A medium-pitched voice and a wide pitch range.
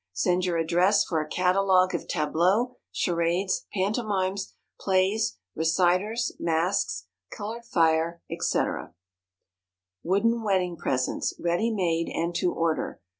No: medium, 180 Hz; average, 3.1 semitones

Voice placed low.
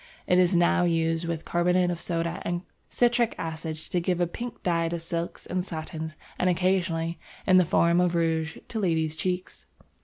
No: medium, 170 Hz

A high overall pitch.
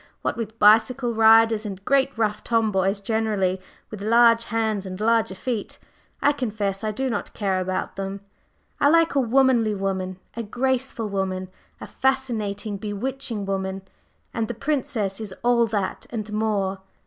Yes: high, 220 Hz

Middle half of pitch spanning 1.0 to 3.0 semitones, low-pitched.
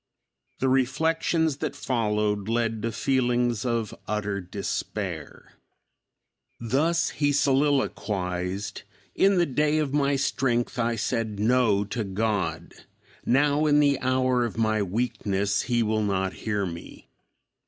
No: average, 4.8 semitones; low, 120 Hz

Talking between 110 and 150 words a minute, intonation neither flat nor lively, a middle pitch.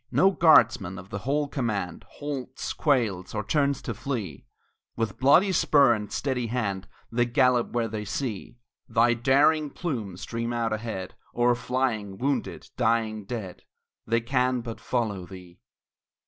No: average, 145 wpm; average, 3.9 semitones; low, 120 Hz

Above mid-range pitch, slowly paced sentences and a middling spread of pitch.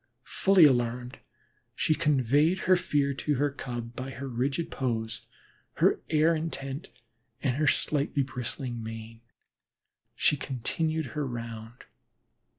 No: low, 135 Hz; slow, 120 wpm; average, 4.0 semitones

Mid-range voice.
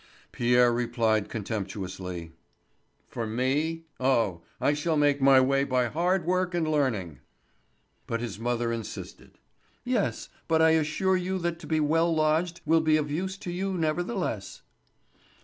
Yes: medium, 150 Hz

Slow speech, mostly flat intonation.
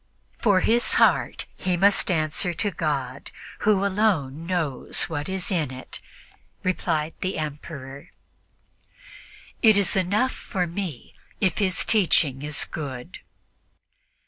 No: slow, 120 wpm; average, 4.7 semitones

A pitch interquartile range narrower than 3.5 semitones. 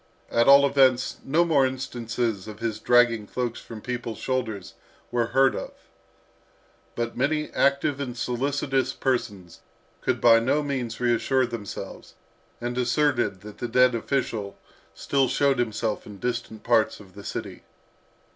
Yes: average, 2.8 semitones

